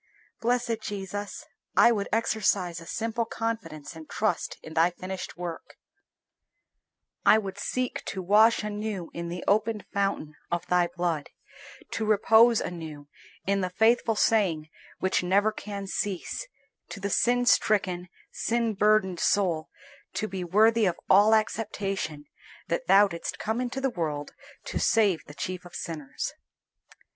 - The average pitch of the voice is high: Yes, high, 200 Hz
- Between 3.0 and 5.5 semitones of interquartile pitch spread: Yes, average, 4.0 semitones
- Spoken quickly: No, average, 140 wpm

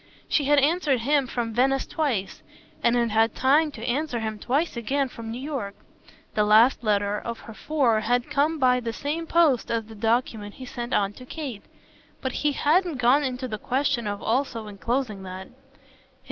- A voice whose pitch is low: No, high, 245 Hz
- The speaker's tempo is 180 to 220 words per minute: Yes, average, 185 wpm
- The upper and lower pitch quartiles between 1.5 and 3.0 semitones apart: No, average, 4.2 semitones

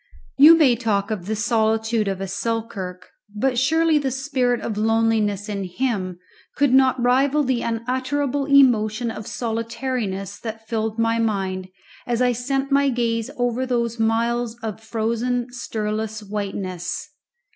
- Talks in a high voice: Yes, high, 230 Hz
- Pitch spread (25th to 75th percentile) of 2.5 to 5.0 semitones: Yes, average, 2.8 semitones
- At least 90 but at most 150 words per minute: Yes, average, 140 wpm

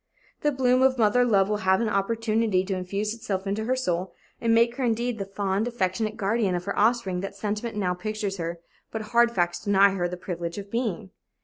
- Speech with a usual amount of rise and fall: Yes, average, 3.4 semitones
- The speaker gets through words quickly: Yes, fast, 210 wpm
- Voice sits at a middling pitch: No, high, 210 Hz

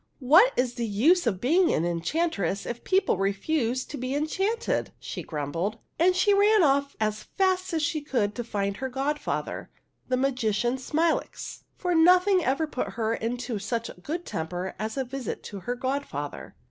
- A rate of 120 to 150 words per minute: No, average, 175 wpm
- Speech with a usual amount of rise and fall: No, wide, 7.1 semitones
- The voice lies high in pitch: Yes, very high, 255 Hz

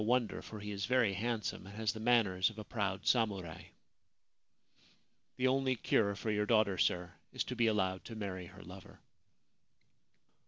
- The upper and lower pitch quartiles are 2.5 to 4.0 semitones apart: Yes, average, 3.2 semitones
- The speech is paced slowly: No, average, 165 wpm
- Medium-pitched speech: No, low, 105 Hz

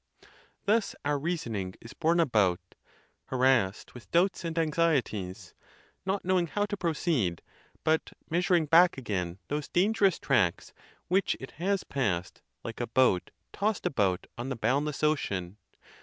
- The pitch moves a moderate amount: No, wide, 8.4 semitones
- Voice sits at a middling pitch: Yes, medium, 150 Hz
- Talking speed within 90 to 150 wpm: Yes, average, 140 wpm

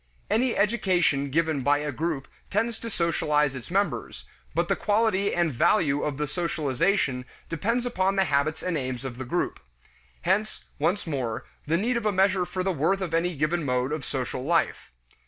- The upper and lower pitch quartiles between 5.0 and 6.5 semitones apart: Yes, wide, 5.5 semitones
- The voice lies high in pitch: No, medium, 165 Hz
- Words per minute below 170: No, average, 180 wpm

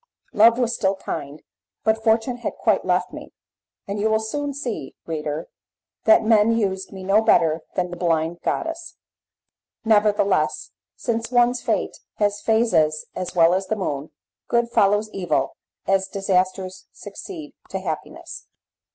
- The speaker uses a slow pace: No, average, 145 wpm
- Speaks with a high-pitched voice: Yes, high, 205 Hz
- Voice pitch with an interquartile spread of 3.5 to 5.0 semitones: Yes, average, 4.2 semitones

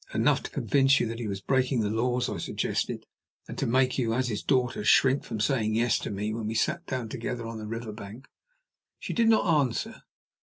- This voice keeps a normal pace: No, fast, 215 wpm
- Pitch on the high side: No, low, 120 Hz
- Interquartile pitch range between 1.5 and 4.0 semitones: Yes, average, 3.2 semitones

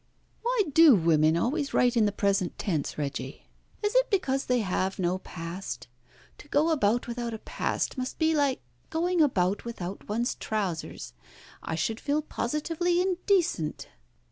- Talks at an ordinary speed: Yes, average, 150 wpm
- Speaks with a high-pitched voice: Yes, high, 235 Hz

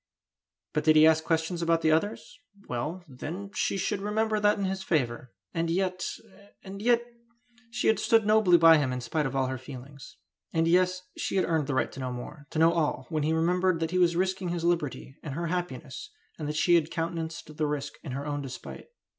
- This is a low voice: No, medium, 165 Hz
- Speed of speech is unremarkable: No, fast, 215 wpm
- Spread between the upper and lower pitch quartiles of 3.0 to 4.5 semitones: Yes, average, 3.7 semitones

